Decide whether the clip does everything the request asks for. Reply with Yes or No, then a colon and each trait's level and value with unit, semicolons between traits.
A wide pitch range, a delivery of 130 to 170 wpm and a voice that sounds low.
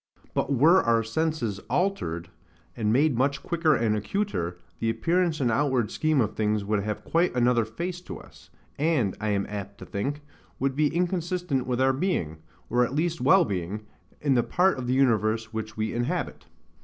No: wide, 6.6 semitones; average, 180 wpm; low, 125 Hz